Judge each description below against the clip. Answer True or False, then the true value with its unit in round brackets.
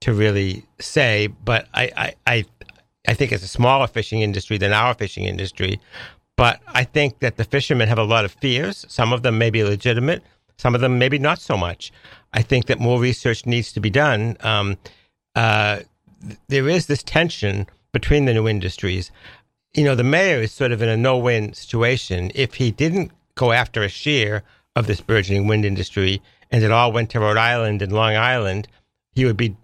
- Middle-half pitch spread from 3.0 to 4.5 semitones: True (3.4 semitones)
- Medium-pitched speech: False (115 Hz)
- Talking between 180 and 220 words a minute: True (200 wpm)